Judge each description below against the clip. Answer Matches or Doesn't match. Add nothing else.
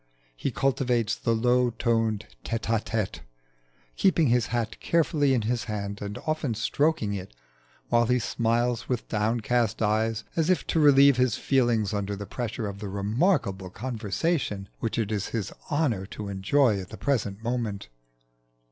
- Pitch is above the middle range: Doesn't match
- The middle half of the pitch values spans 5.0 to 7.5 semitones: Doesn't match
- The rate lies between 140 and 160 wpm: Matches